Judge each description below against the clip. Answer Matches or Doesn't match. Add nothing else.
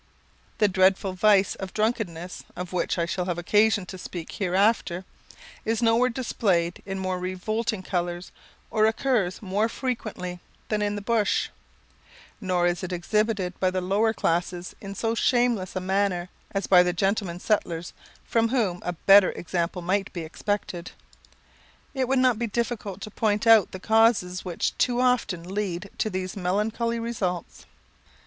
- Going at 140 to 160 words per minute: Matches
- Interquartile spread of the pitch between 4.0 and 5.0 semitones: Doesn't match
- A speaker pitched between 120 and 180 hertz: Doesn't match